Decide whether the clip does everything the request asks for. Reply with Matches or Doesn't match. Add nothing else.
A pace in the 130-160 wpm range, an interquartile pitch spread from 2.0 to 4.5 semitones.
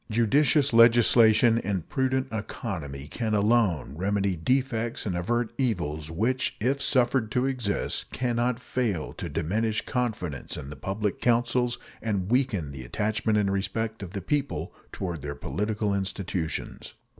Matches